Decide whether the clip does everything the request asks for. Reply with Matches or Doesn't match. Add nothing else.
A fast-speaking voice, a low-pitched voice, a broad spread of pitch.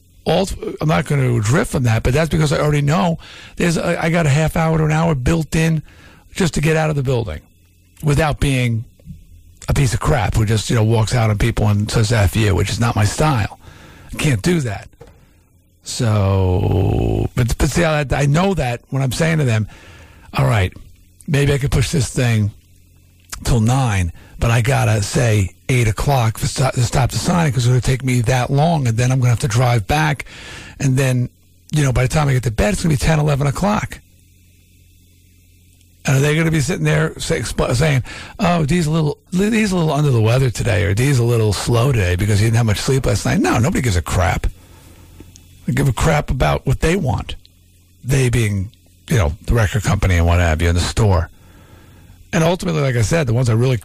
Matches